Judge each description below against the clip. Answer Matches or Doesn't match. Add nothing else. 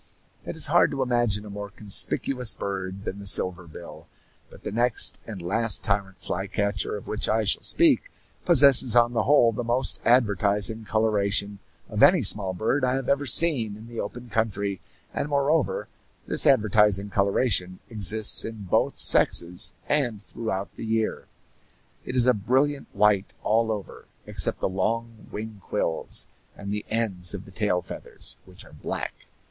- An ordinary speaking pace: Matches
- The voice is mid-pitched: Doesn't match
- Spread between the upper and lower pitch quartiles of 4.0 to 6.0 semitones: Doesn't match